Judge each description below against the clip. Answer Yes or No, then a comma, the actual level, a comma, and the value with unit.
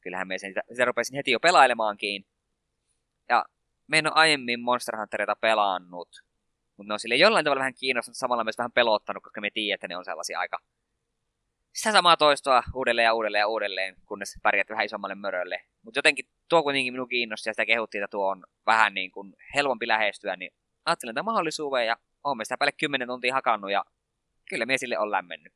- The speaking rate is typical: No, fast, 195 wpm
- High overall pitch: No, low, 115 Hz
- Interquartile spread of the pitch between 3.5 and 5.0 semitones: Yes, average, 4.0 semitones